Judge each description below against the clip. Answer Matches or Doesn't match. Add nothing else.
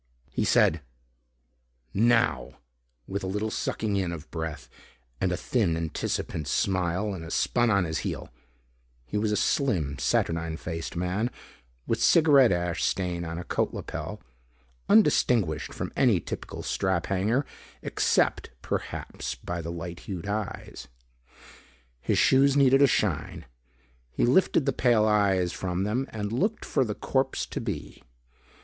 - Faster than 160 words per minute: Doesn't match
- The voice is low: Matches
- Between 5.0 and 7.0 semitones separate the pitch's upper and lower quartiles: Matches